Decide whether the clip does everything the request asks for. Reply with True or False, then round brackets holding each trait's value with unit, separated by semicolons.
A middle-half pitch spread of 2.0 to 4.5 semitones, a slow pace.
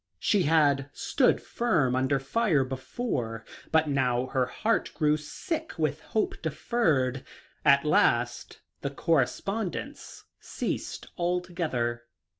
False (5.6 semitones; 105 wpm)